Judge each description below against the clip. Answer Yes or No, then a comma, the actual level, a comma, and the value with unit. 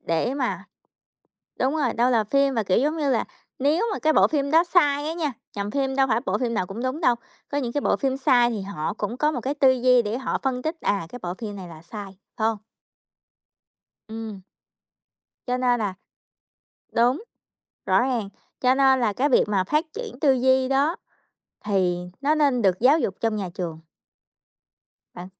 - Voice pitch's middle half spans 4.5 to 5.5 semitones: Yes, average, 5.0 semitones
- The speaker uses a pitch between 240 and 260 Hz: Yes, very high, 250 Hz